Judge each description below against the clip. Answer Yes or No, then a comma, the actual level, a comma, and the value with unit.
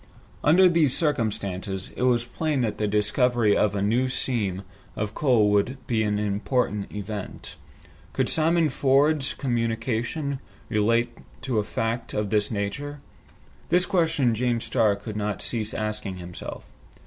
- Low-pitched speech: Yes, low, 115 Hz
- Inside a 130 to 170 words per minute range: Yes, average, 140 wpm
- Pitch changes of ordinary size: Yes, average, 4.0 semitones